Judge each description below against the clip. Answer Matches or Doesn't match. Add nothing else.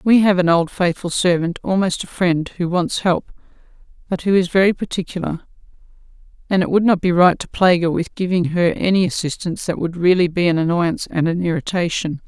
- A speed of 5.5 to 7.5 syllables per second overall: Matches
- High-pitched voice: Doesn't match